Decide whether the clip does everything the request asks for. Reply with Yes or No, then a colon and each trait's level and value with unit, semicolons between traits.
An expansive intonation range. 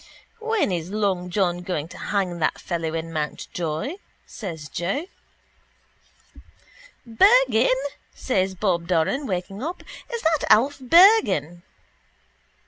Yes: wide, 7.8 semitones